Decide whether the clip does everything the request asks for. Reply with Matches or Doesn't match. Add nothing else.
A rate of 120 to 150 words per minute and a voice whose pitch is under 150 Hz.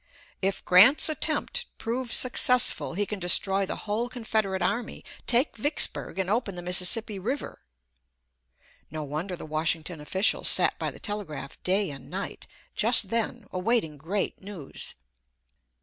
Doesn't match